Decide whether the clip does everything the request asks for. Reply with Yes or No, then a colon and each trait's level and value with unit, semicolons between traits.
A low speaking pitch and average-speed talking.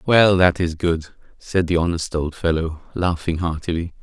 Yes: very low, 85 Hz; average, 165 wpm